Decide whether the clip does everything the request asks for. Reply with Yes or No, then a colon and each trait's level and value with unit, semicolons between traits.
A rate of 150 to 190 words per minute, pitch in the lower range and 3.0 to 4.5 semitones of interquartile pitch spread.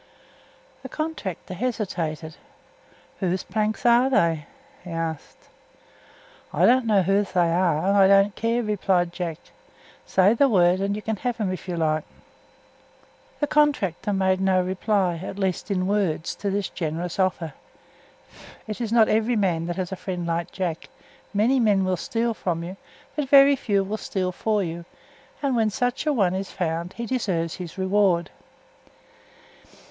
No: average, 160 wpm; high, 195 Hz; average, 3.8 semitones